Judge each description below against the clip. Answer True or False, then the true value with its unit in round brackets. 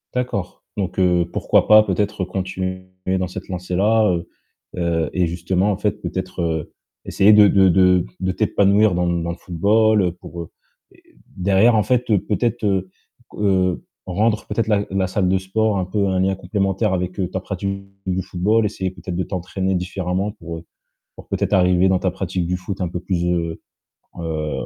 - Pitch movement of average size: False (2.2 semitones)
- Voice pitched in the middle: False (95 Hz)